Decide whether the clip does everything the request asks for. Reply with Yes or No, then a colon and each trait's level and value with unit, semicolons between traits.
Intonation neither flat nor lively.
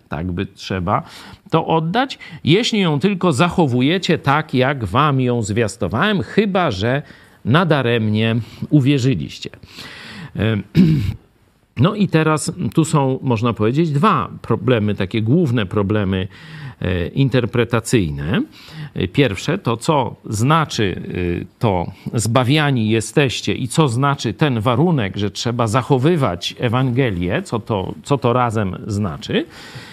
No: wide, 6.0 semitones